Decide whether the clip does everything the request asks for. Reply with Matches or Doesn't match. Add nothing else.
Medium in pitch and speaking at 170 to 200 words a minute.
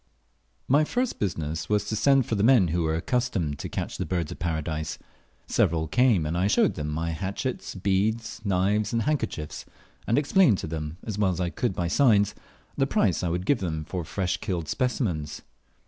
Doesn't match